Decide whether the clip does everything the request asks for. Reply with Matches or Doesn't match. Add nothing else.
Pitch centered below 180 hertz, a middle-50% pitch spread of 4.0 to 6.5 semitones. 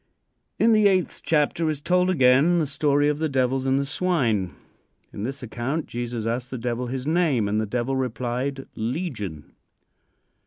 Matches